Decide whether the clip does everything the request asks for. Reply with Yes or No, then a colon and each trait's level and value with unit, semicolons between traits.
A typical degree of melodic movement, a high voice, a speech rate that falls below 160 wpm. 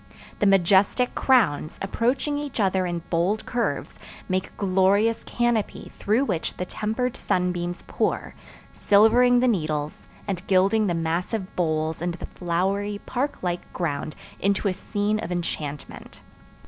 Yes: average, 4.1 semitones; high, 195 Hz; slow, 135 wpm